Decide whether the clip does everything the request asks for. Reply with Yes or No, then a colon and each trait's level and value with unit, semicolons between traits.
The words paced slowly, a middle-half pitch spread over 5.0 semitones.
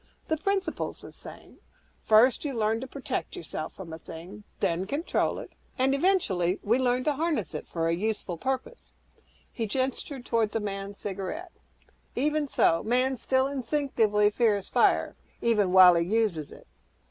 No: average, 160 wpm; wide, 5.6 semitones